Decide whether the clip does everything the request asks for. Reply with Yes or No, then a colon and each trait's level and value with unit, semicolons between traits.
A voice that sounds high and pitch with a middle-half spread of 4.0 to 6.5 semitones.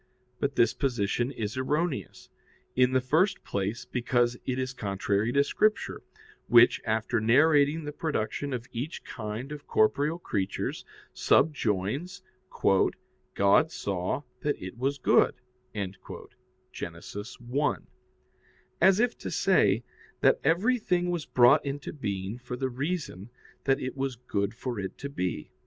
No: low, 130 Hz; average, 5.1 semitones